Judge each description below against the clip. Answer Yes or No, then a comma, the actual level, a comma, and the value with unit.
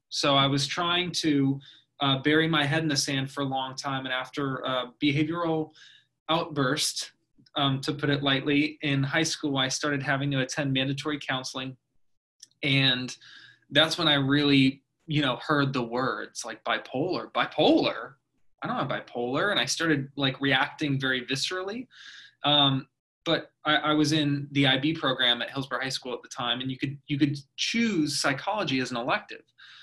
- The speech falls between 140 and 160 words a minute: No, average, 175 wpm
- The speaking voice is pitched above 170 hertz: No, medium, 140 Hz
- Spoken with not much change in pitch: Yes, narrow, 2.3 semitones